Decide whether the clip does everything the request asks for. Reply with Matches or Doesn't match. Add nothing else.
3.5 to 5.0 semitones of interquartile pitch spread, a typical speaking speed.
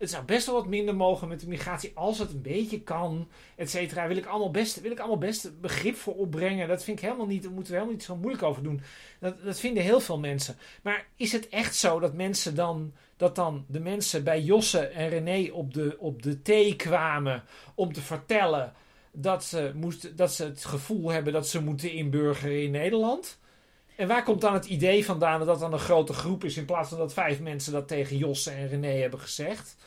Doesn't match